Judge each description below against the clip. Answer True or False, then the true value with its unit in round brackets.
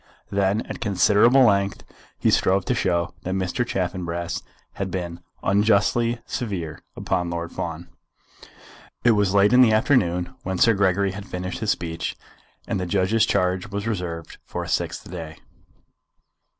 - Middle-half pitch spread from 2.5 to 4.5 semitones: True (2.8 semitones)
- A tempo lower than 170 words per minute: True (150 wpm)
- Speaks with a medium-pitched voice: False (95 Hz)